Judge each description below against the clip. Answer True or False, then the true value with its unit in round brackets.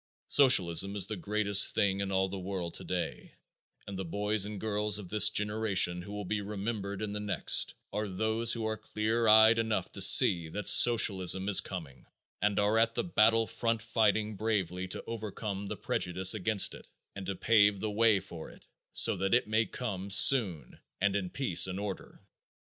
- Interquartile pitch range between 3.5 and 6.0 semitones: False (2.4 semitones)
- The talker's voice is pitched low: True (105 Hz)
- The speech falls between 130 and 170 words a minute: False (185 wpm)